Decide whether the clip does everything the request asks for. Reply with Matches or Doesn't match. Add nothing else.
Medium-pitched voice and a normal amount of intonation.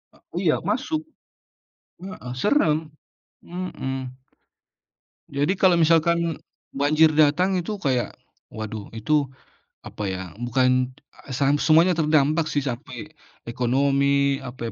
Matches